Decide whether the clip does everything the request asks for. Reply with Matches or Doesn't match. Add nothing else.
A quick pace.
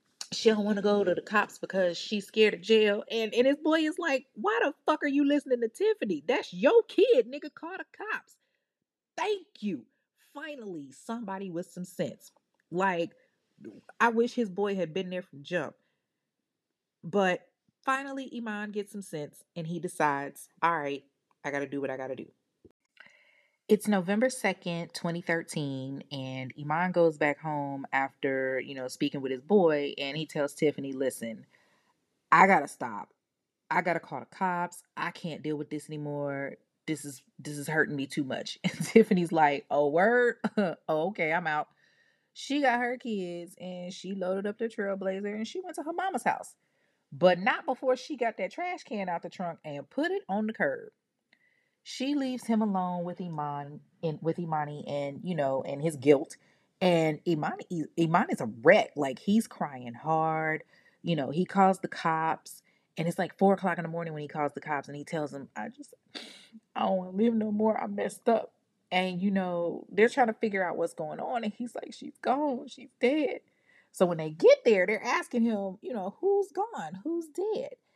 Doesn't match